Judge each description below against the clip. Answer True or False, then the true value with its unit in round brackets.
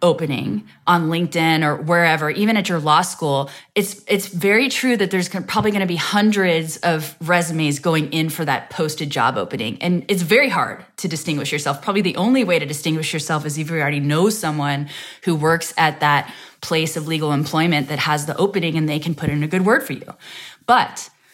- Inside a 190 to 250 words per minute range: True (205 wpm)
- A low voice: False (165 Hz)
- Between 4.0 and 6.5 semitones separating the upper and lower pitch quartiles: False (3.5 semitones)